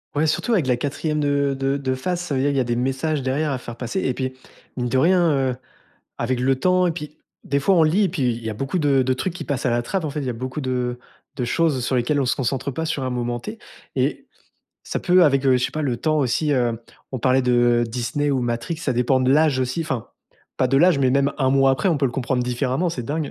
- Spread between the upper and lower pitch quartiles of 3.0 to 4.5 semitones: Yes, average, 3.3 semitones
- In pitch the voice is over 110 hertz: Yes, low, 135 Hz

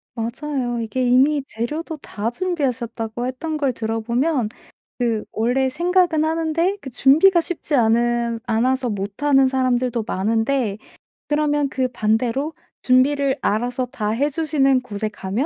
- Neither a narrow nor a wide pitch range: Yes, average, 4.3 semitones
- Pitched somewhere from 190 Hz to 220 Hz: No, very high, 255 Hz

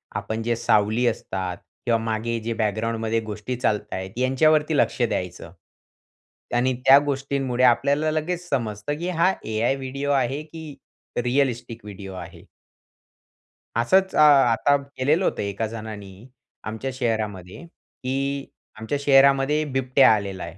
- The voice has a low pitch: Yes, low, 120 Hz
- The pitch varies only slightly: No, average, 4.1 semitones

